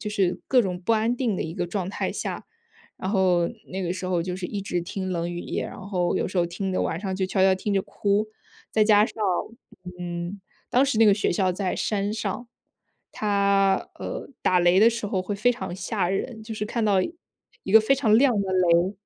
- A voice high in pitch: Yes, high, 195 Hz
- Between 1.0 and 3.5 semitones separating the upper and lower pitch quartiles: Yes, average, 2.8 semitones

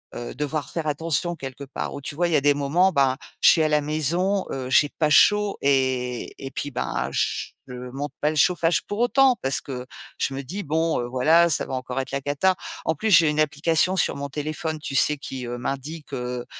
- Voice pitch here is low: No, medium, 150 Hz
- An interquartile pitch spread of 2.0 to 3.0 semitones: No, average, 3.5 semitones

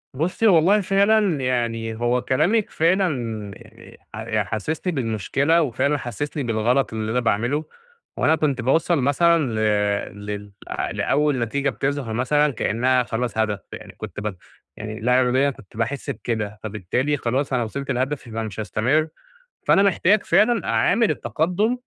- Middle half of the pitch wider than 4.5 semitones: Yes, wide, 5.6 semitones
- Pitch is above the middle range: No, low, 130 Hz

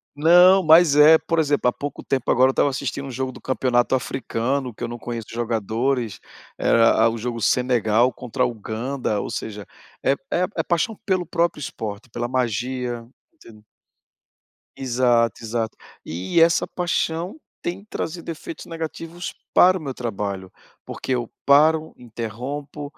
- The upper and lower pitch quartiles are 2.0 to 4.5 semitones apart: No, average, 5.3 semitones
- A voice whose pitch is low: Yes, low, 130 Hz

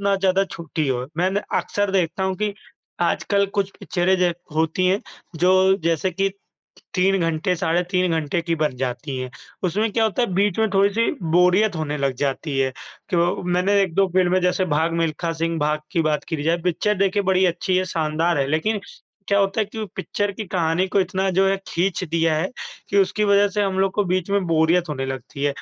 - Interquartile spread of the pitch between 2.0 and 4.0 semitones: Yes, average, 3.3 semitones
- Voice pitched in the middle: Yes, medium, 180 Hz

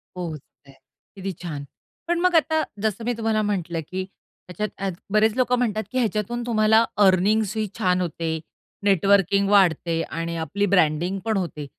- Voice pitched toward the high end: Yes, high, 200 Hz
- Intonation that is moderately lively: Yes, average, 3.9 semitones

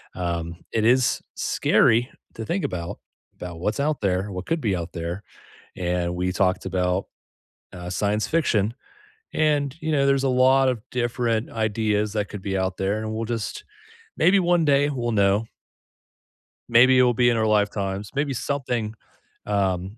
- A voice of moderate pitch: No, low, 110 Hz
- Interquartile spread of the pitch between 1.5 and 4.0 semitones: No, average, 5.0 semitones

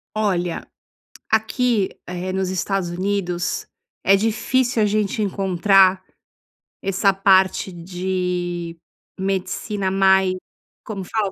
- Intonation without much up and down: Yes, narrow, 1.9 semitones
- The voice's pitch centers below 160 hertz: No, high, 190 Hz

